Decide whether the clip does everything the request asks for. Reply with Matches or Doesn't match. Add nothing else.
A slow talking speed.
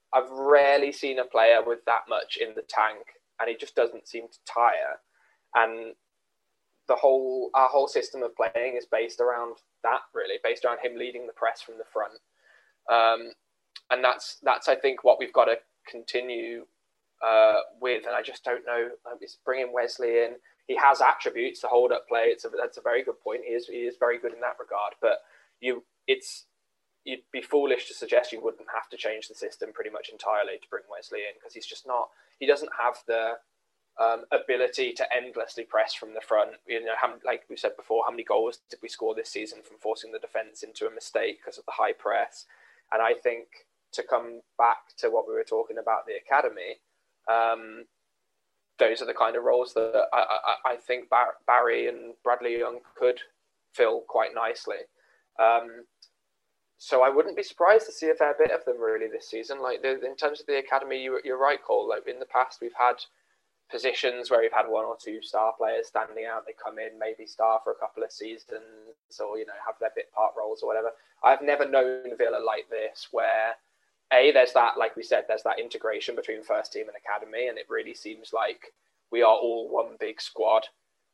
Doesn't match